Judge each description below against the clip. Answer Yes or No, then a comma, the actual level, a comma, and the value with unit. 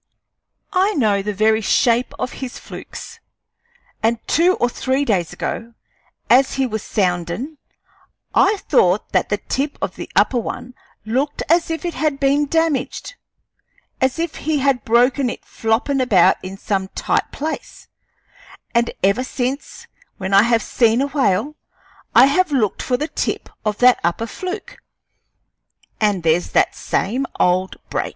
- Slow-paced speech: No, average, 150 wpm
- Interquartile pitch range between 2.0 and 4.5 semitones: No, average, 5.1 semitones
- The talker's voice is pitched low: No, very high, 250 Hz